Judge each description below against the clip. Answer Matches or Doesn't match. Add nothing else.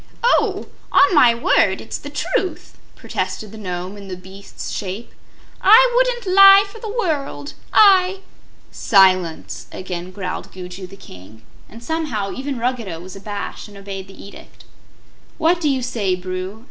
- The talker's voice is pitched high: Matches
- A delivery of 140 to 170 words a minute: Matches